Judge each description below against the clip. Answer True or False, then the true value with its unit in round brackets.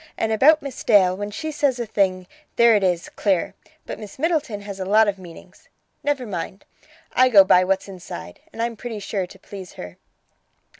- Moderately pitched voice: False (205 Hz)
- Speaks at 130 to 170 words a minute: False (195 wpm)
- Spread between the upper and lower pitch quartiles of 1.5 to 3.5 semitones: False (4.1 semitones)